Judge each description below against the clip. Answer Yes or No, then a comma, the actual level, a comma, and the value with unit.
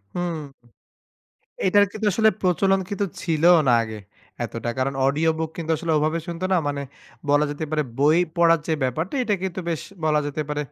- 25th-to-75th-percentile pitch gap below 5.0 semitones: Yes, average, 3.4 semitones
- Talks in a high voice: No, medium, 160 Hz